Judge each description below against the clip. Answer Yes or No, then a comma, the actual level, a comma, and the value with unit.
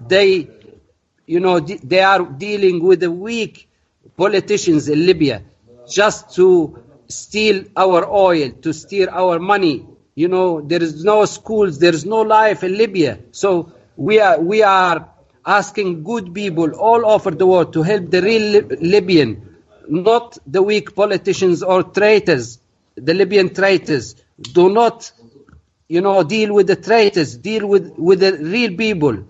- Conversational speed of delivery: Yes, average, 150 wpm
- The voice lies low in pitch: No, medium, 185 Hz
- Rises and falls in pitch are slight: No, average, 4.0 semitones